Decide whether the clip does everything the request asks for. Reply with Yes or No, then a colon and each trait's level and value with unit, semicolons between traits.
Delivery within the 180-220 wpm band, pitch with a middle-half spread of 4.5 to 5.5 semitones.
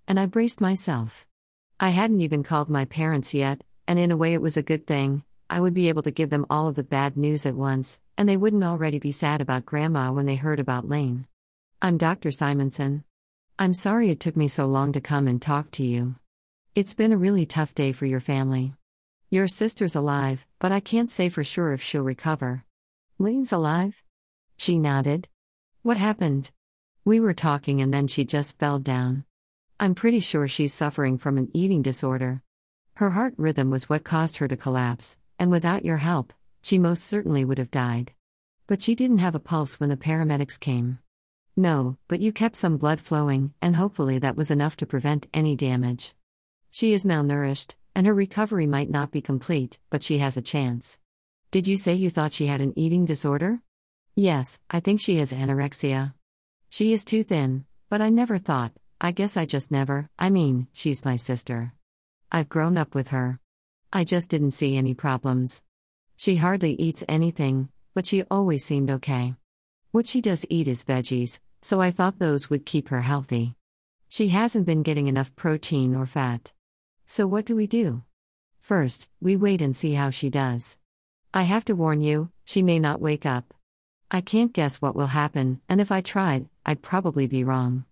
Yes: average, 190 wpm; average, 5.1 semitones